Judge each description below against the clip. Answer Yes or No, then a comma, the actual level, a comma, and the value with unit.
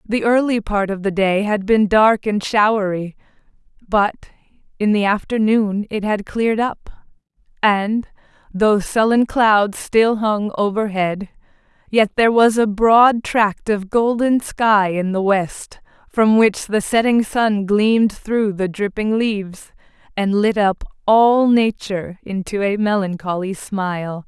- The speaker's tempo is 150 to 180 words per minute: No, average, 140 wpm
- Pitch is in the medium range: No, high, 210 Hz